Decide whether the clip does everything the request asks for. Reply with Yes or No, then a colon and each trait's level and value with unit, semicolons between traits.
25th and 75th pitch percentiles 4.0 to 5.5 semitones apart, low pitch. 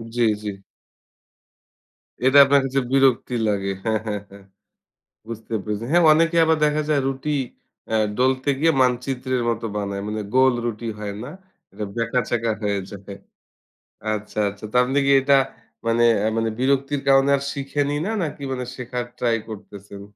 Yes: average, 4.3 semitones; low, 125 Hz